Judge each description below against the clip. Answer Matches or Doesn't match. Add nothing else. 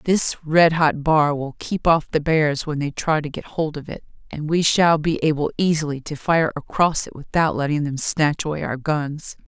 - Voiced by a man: Doesn't match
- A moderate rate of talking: Doesn't match